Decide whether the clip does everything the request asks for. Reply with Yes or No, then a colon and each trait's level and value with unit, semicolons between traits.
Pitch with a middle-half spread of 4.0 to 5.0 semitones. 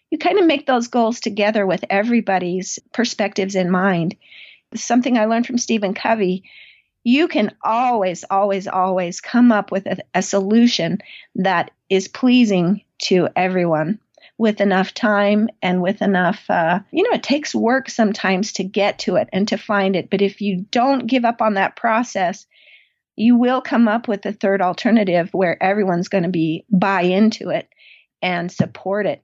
No: average, 3.6 semitones